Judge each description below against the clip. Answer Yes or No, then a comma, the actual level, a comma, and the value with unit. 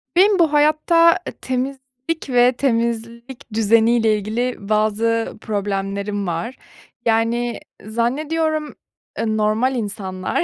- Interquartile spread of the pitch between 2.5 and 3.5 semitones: No, average, 3.9 semitones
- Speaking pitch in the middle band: No, high, 235 Hz